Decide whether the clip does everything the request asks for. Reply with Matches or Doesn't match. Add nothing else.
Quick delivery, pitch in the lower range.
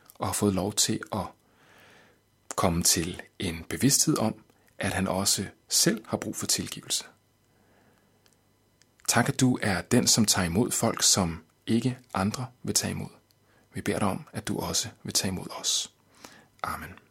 Doesn't match